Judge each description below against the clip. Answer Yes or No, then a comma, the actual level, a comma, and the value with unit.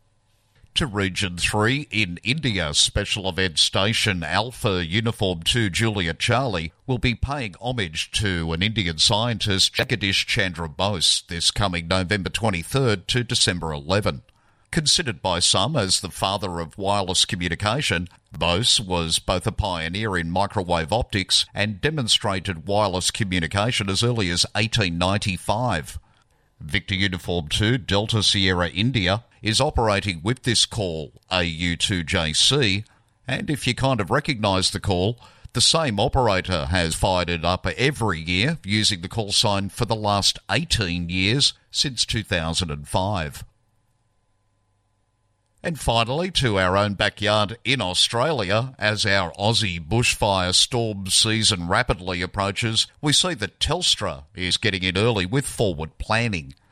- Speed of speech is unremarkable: No, slow, 130 wpm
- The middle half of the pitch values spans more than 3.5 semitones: Yes, average, 3.9 semitones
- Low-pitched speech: Yes, low, 100 Hz